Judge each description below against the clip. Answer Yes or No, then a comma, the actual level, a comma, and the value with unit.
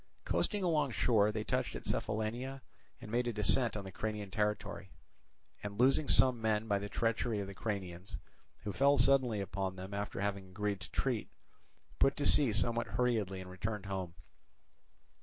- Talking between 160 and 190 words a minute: Yes, average, 170 wpm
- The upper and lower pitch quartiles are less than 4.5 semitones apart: Yes, average, 3.5 semitones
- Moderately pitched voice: No, low, 105 Hz